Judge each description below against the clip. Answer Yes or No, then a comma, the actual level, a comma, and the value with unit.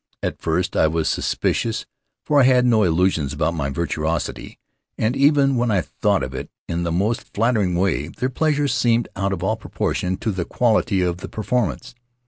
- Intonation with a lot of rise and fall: Yes, wide, 6.3 semitones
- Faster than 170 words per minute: Yes, average, 185 wpm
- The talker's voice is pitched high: No, low, 100 Hz